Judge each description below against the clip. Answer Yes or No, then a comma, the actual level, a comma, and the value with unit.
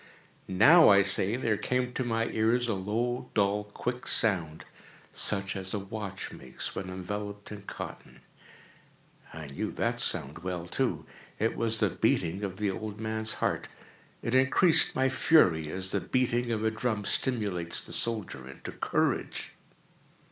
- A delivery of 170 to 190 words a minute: No, average, 155 wpm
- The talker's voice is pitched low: Yes, low, 105 Hz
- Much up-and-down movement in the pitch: No, average, 3.7 semitones